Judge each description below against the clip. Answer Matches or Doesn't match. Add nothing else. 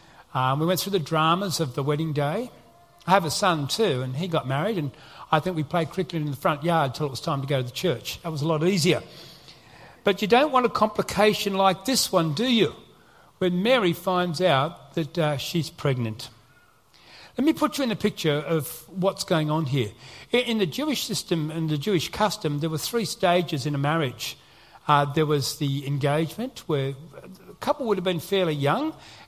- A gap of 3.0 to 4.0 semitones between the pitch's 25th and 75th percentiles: Doesn't match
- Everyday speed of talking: Doesn't match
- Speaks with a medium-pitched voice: Matches